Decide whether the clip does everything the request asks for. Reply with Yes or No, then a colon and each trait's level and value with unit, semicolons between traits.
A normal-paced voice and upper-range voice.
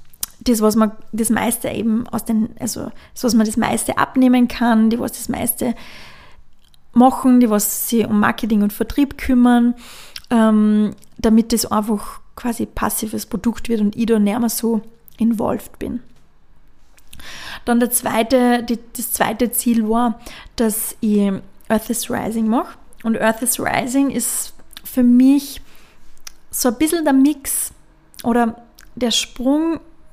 Yes: average, 145 wpm; high, 230 Hz